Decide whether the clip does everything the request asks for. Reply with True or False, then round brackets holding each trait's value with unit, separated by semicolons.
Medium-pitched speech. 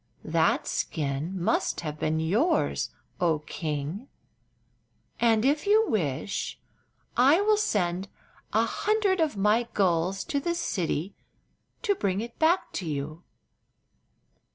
False (200 Hz)